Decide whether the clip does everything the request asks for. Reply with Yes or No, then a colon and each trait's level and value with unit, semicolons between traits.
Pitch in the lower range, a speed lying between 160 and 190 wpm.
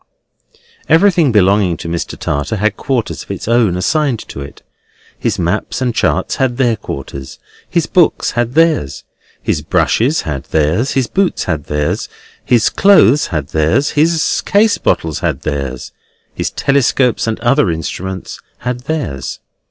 No: low, 115 Hz; average, 145 wpm